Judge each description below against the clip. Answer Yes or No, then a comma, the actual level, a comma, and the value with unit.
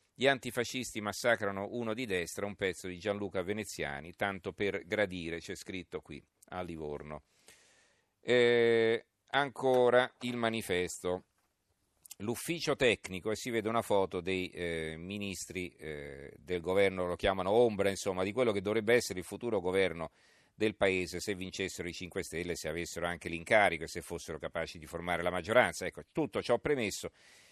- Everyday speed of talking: Yes, average, 155 wpm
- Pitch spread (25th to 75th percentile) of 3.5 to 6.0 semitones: Yes, average, 4.1 semitones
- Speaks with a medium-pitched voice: No, very low, 95 Hz